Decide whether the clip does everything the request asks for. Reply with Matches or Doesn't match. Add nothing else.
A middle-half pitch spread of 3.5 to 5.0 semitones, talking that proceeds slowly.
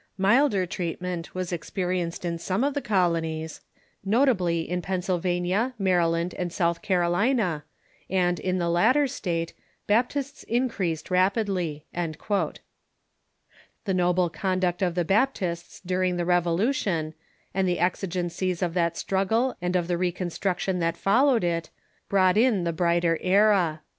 Doesn't match